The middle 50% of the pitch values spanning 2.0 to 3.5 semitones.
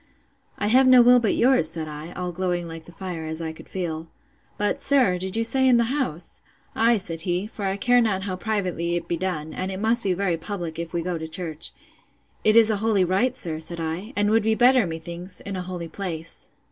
No: average, 4.7 semitones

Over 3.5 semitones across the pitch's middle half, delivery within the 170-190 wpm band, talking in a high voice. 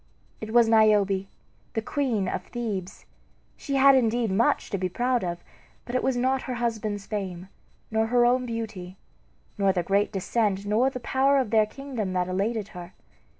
Yes: average, 3.9 semitones; average, 175 wpm; high, 220 Hz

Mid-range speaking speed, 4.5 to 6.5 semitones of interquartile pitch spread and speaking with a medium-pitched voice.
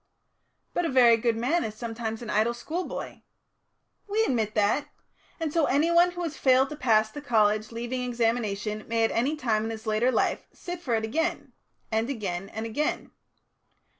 No: average, 170 wpm; average, 4.9 semitones; high, 235 Hz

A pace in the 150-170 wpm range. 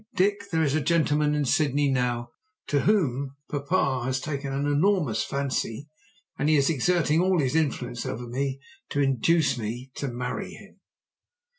Yes: average, 160 wpm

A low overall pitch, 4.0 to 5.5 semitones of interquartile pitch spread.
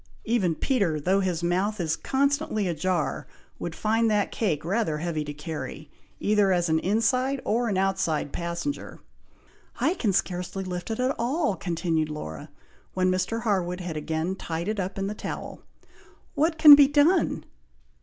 No: high, 190 Hz; average, 5.1 semitones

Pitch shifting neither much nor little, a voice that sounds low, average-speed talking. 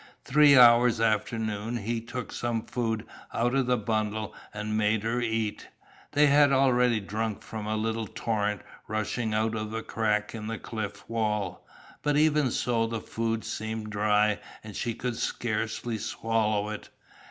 No: narrow, 1.8 semitones; low, 110 Hz; average, 160 wpm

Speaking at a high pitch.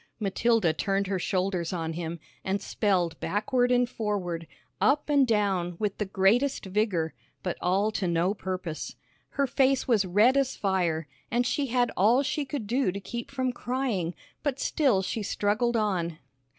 Yes: high, 205 Hz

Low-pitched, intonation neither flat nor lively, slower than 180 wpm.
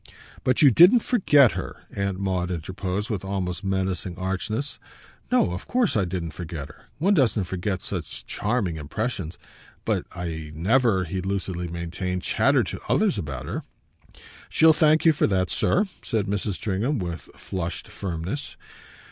Yes: very low, 95 Hz; average, 4.7 semitones; average, 155 wpm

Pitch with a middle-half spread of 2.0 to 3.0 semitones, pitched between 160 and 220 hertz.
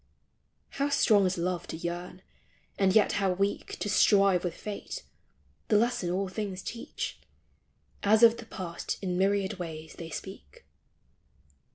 Yes: narrow, 2.6 semitones; high, 190 Hz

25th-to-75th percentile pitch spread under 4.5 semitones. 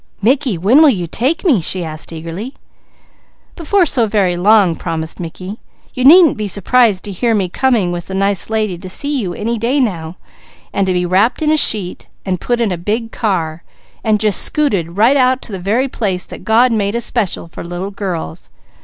No: average, 5.2 semitones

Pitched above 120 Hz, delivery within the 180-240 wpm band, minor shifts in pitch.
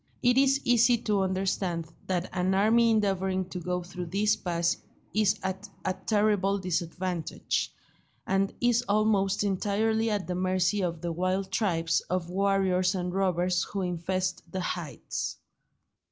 No: high, 190 Hz; average, 140 wpm; narrow, 2.3 semitones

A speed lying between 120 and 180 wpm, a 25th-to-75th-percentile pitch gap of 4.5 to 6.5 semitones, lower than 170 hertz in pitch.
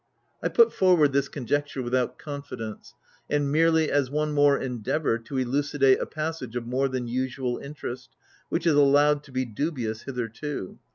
No: average, 160 wpm; average, 2.9 semitones; medium, 140 Hz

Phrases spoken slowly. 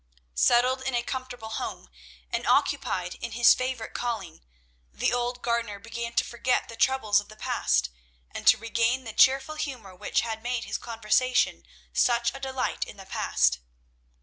No: average, 165 wpm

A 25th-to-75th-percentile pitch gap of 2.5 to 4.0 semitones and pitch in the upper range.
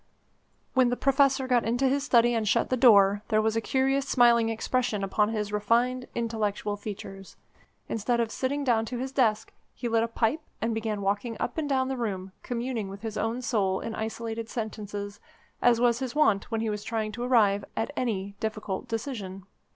Yes: average, 3.0 semitones; high, 225 Hz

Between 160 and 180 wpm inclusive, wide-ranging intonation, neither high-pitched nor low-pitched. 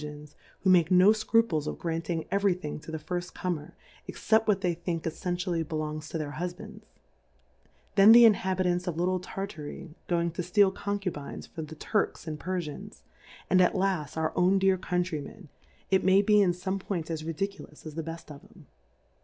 No: average, 170 wpm; average, 3.2 semitones; medium, 175 Hz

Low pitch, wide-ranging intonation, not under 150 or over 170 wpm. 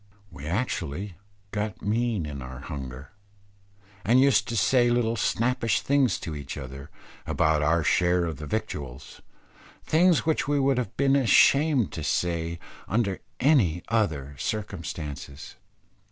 No: very low, 95 Hz; wide, 8.3 semitones; slow, 135 wpm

